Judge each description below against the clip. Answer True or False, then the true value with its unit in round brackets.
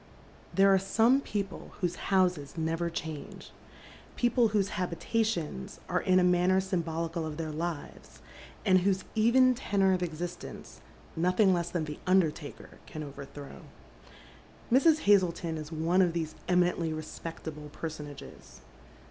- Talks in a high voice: False (175 Hz)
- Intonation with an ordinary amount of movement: True (3.3 semitones)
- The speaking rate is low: True (130 wpm)